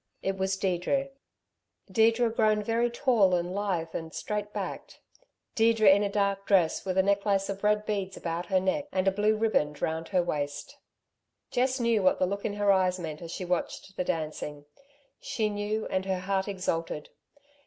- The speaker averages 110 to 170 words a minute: No, average, 180 wpm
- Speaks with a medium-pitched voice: No, high, 195 Hz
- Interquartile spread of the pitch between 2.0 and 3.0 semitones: Yes, average, 2.7 semitones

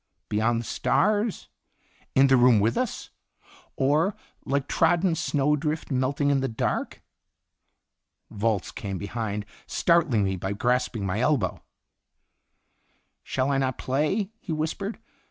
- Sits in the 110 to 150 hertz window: Yes, low, 135 Hz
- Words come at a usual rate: No, slow, 120 wpm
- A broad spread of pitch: Yes, wide, 5.7 semitones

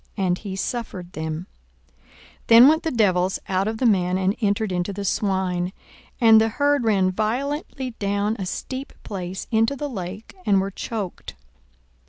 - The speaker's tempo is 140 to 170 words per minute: Yes, average, 165 wpm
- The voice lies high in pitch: Yes, high, 200 Hz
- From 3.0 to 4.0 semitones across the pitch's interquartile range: Yes, average, 3.5 semitones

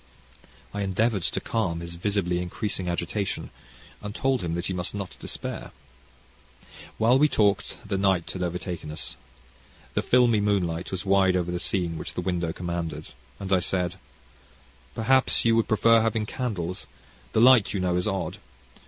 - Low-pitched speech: Yes, very low, 95 Hz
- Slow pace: No, average, 160 wpm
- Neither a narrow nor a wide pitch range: Yes, average, 3.5 semitones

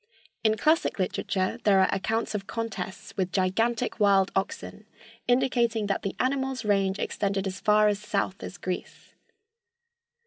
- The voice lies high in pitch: Yes, high, 205 Hz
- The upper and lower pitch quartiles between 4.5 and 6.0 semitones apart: No, average, 2.9 semitones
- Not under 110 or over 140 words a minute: Yes, slow, 135 wpm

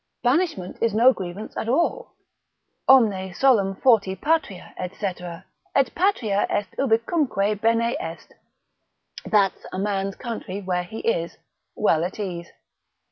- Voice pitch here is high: Yes, high, 210 Hz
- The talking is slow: Yes, slow, 125 wpm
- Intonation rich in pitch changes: No, average, 4.6 semitones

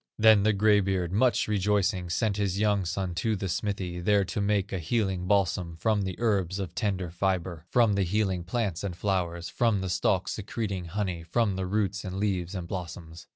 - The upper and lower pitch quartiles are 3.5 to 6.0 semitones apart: No, narrow, 2.6 semitones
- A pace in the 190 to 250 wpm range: Yes, average, 195 wpm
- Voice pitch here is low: Yes, very low, 95 Hz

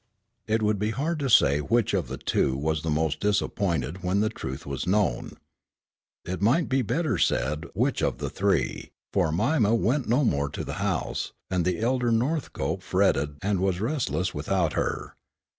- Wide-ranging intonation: Yes, wide, 6.8 semitones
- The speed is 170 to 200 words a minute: Yes, average, 175 wpm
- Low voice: Yes, very low, 95 Hz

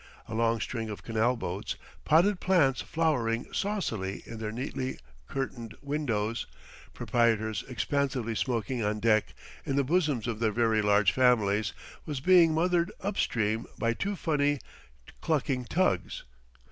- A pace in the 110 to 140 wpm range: Yes, slow, 135 wpm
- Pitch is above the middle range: No, low, 120 Hz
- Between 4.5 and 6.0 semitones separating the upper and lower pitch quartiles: Yes, average, 5.1 semitones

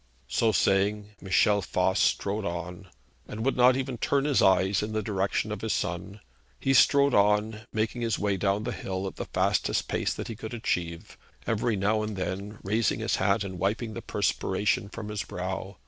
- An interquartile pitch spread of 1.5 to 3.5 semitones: Yes, narrow, 2.5 semitones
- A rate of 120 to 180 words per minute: No, average, 190 wpm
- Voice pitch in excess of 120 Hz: No, low, 105 Hz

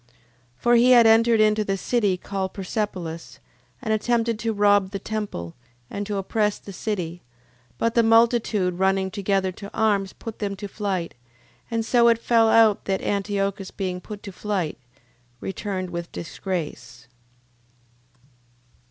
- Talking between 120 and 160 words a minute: Yes, average, 145 wpm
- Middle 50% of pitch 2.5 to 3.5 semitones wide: Yes, average, 2.8 semitones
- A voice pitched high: Yes, high, 200 Hz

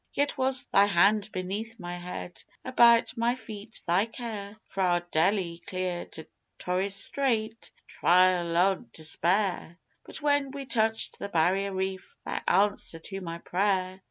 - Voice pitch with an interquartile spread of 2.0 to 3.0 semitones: No, average, 3.8 semitones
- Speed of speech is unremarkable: Yes, average, 145 wpm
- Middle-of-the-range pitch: No, high, 195 Hz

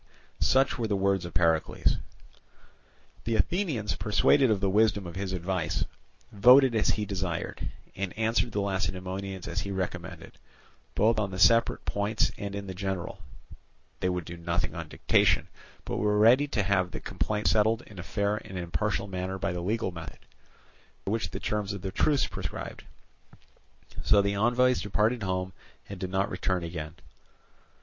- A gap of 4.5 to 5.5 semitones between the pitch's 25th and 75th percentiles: No, average, 2.7 semitones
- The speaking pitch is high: No, low, 100 Hz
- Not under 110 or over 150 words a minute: No, average, 165 wpm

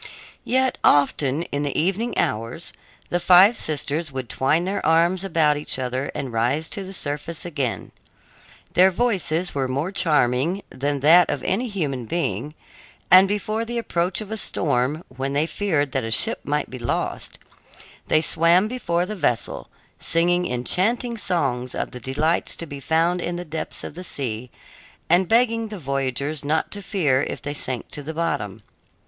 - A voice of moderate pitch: Yes, medium, 160 Hz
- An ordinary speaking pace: Yes, average, 170 wpm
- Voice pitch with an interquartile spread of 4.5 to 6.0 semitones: Yes, average, 5.1 semitones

